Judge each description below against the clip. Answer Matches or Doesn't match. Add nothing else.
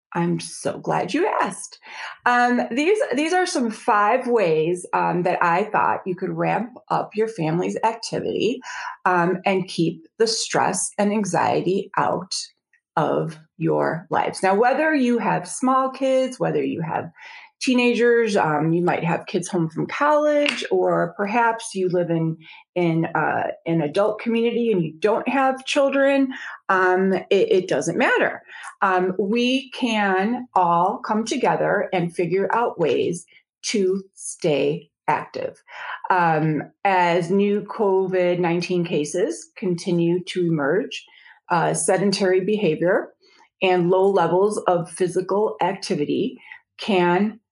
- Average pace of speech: Doesn't match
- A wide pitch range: Matches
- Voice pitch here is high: Matches